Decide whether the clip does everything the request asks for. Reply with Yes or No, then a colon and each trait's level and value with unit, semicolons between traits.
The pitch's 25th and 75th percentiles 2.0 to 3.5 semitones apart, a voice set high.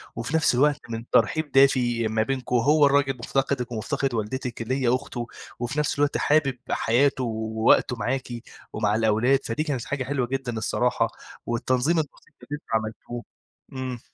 No: average, 3.0 semitones; low, 125 Hz